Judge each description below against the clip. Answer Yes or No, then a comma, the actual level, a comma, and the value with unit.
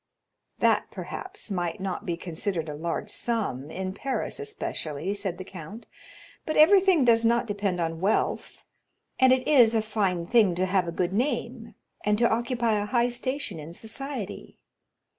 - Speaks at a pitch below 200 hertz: No, high, 210 Hz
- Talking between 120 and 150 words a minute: No, average, 160 wpm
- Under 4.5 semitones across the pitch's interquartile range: No, average, 5.3 semitones